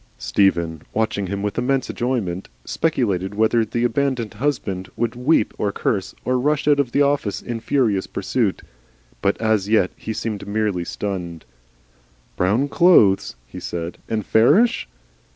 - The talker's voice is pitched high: No, low, 110 Hz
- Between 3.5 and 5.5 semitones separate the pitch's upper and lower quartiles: Yes, average, 4.4 semitones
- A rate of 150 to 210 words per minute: No, average, 140 wpm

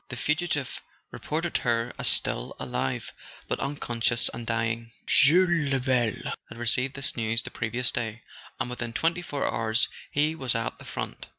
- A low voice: Yes, low, 125 Hz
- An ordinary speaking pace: Yes, average, 160 wpm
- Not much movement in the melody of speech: No, average, 4.0 semitones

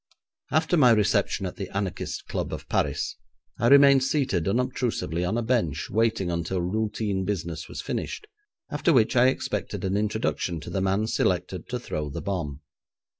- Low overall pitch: Yes, low, 100 Hz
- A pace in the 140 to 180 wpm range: Yes, average, 165 wpm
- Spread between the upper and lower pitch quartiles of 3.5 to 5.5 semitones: Yes, average, 5.2 semitones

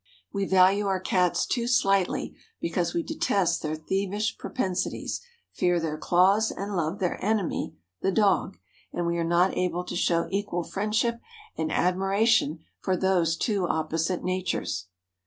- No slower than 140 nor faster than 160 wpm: Yes, average, 145 wpm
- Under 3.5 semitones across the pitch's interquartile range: Yes, narrow, 2.6 semitones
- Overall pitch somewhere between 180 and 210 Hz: Yes, medium, 185 Hz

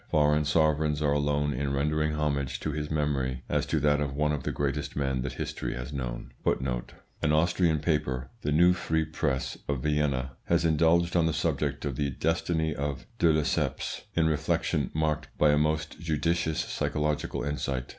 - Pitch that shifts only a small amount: Yes, narrow, 1.7 semitones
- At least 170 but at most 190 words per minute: Yes, average, 175 wpm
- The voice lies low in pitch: Yes, very low, 75 Hz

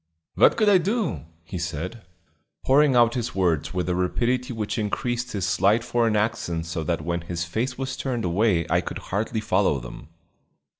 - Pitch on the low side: Yes, low, 105 Hz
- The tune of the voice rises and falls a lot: Yes, wide, 6.0 semitones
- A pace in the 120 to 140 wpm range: No, average, 180 wpm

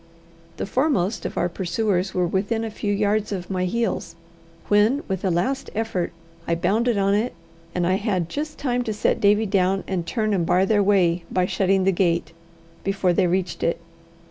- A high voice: Yes, high, 195 Hz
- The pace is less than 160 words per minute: No, average, 190 wpm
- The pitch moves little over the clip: No, average, 3.0 semitones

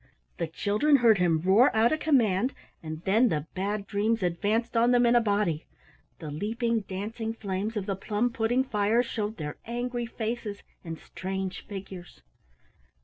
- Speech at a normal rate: Yes, average, 160 wpm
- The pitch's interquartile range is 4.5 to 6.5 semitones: No, average, 3.7 semitones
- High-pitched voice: Yes, high, 210 Hz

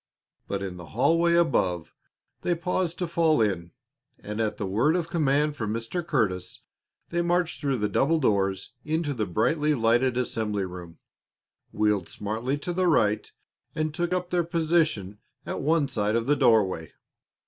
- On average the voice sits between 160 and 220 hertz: No, low, 130 Hz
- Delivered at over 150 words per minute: Yes, average, 160 wpm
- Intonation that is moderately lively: No, wide, 8.0 semitones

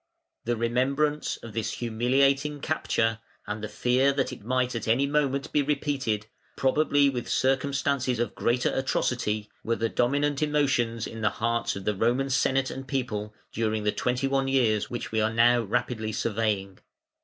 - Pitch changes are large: No, average, 3.4 semitones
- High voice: No, low, 125 Hz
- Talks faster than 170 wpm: No, average, 165 wpm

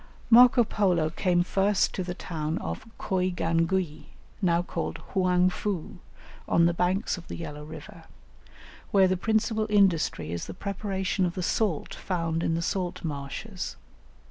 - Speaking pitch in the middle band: Yes, medium, 180 Hz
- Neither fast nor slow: Yes, average, 145 wpm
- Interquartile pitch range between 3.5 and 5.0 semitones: No, average, 2.8 semitones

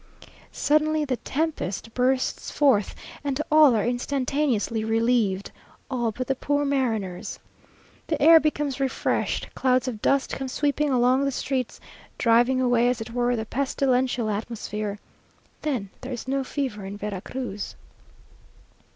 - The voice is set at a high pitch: Yes, very high, 255 Hz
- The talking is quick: No, slow, 135 wpm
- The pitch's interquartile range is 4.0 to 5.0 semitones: No, average, 3.5 semitones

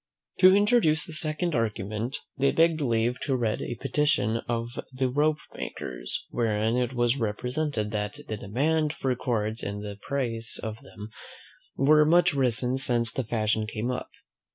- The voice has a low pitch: Yes, low, 125 Hz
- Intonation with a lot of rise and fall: No, average, 5.0 semitones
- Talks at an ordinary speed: Yes, average, 155 wpm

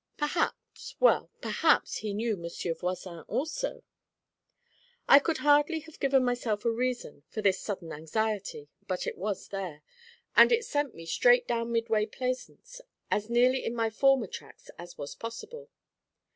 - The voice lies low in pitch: No, high, 230 Hz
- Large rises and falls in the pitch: Yes, wide, 6.1 semitones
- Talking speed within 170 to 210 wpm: No, average, 150 wpm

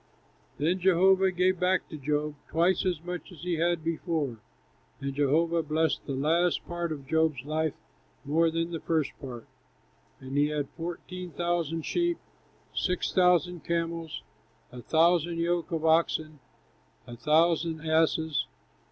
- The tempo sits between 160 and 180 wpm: No, average, 145 wpm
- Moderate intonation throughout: No, narrow, 2.3 semitones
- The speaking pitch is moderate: Yes, medium, 165 Hz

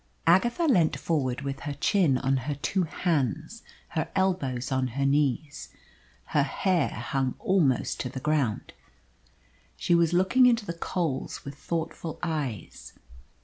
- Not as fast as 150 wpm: Yes, average, 140 wpm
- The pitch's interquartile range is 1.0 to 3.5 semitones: No, average, 4.7 semitones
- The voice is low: No, medium, 150 Hz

